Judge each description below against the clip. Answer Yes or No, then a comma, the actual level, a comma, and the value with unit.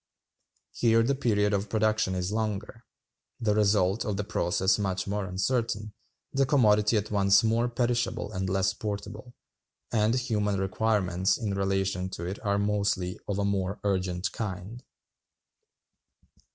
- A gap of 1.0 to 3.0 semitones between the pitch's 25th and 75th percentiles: Yes, narrow, 2.4 semitones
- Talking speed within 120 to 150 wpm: Yes, average, 140 wpm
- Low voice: Yes, low, 105 Hz